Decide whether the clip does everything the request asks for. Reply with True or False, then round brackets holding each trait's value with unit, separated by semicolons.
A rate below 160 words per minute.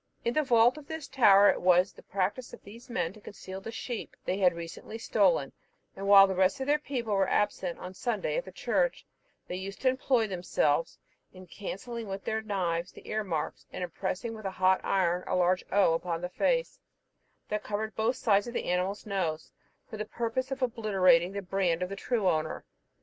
False (205 wpm)